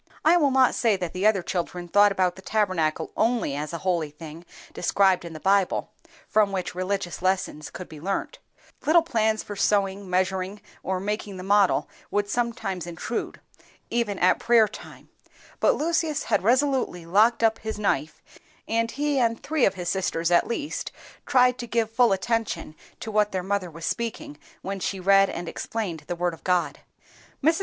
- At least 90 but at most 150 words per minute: No, average, 175 wpm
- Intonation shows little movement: No, average, 4.2 semitones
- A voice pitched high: Yes, high, 200 Hz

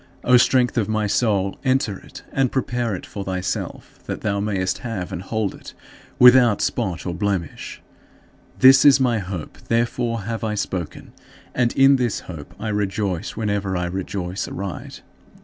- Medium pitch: No, low, 105 Hz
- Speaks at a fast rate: No, average, 160 wpm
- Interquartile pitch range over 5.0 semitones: No, average, 4.2 semitones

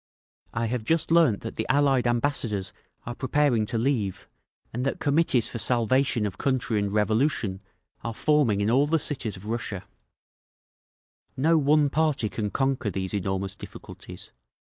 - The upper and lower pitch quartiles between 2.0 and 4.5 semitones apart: No, average, 5.1 semitones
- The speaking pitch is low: Yes, low, 120 Hz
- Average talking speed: Yes, average, 150 wpm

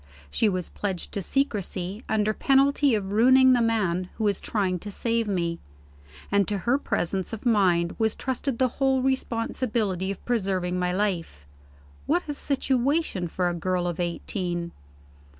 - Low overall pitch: No, high, 205 Hz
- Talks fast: No, average, 155 wpm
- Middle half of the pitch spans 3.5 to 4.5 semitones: No, average, 5.2 semitones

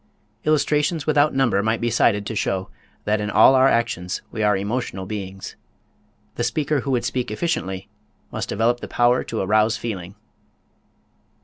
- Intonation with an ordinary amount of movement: Yes, average, 4.3 semitones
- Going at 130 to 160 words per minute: Yes, average, 155 wpm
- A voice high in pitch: No, low, 115 Hz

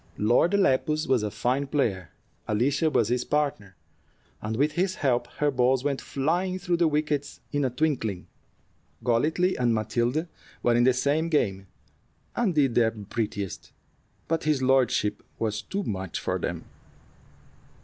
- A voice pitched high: No, low, 130 Hz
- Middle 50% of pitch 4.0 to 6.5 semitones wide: Yes, average, 5.1 semitones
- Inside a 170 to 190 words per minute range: No, average, 150 wpm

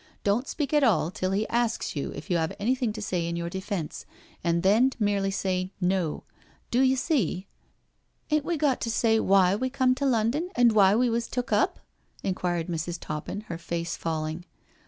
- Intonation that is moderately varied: No, wide, 5.8 semitones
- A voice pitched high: Yes, high, 200 Hz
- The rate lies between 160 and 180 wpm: No, average, 200 wpm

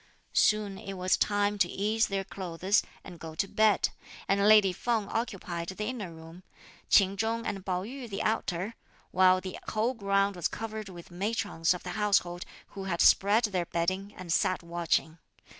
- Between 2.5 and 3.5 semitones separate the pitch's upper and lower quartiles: Yes, average, 2.9 semitones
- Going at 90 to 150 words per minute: No, average, 175 wpm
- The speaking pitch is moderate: No, high, 195 Hz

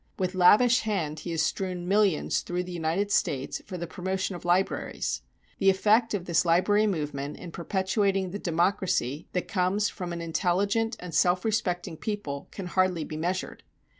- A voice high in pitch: No, medium, 180 Hz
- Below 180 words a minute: Yes, average, 165 wpm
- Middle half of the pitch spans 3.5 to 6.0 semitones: No, average, 2.8 semitones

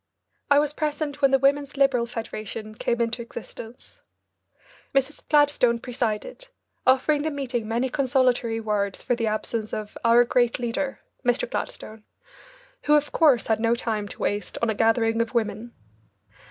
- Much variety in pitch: No, average, 3.4 semitones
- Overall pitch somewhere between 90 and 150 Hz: No, high, 240 Hz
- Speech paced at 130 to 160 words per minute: Yes, average, 155 wpm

